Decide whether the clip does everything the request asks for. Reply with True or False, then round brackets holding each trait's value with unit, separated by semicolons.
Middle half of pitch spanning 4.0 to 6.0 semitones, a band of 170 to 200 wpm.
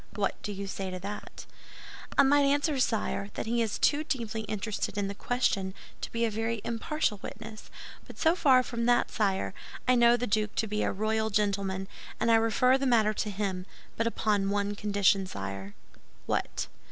False (2.9 semitones; 185 wpm)